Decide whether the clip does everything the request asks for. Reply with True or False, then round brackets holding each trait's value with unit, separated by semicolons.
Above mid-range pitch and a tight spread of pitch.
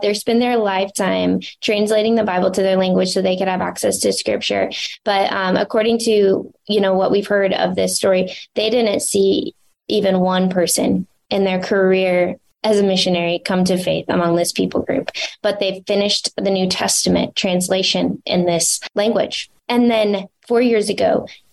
True (195 Hz; 2.2 semitones)